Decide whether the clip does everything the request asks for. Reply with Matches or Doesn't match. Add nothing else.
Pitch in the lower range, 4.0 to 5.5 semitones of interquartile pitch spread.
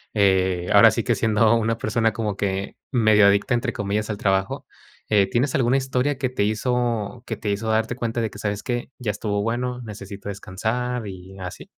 Doesn't match